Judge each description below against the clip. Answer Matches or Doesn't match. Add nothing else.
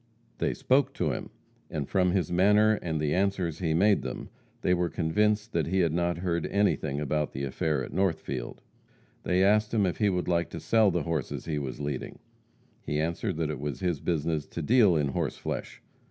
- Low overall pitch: Matches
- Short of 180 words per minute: Doesn't match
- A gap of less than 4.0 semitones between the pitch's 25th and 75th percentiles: Doesn't match